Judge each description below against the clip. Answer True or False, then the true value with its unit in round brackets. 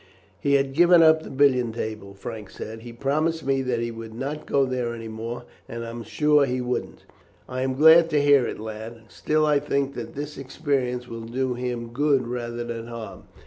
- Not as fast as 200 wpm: False (205 wpm)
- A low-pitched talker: True (125 Hz)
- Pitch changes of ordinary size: True (3.4 semitones)